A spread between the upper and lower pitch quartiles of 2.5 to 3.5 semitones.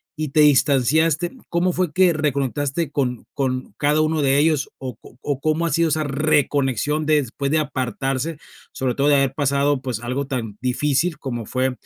Yes: average, 2.8 semitones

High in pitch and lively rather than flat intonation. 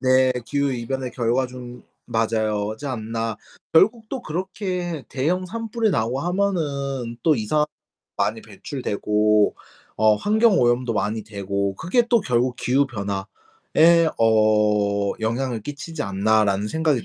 No: low, 125 Hz; wide, 6.9 semitones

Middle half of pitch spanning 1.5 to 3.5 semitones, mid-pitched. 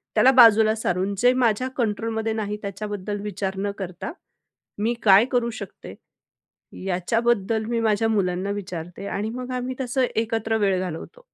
No: average, 2.8 semitones; high, 215 Hz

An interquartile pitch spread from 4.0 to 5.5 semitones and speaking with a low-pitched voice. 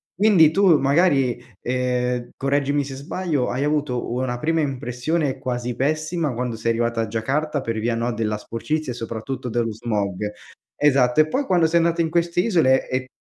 Yes: average, 4.4 semitones; low, 130 Hz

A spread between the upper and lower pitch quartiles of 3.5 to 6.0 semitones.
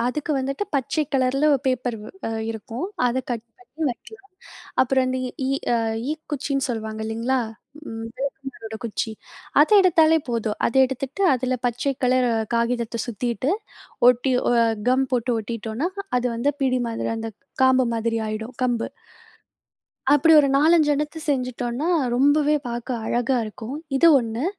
No: average, 3.0 semitones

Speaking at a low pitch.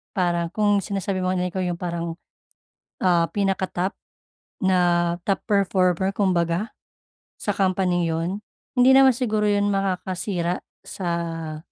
No: medium, 185 Hz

